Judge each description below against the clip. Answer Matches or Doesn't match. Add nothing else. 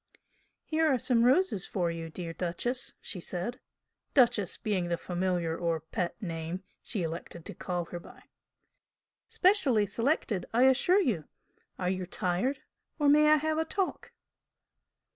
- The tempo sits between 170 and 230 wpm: Doesn't match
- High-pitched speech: Matches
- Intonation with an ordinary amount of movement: Doesn't match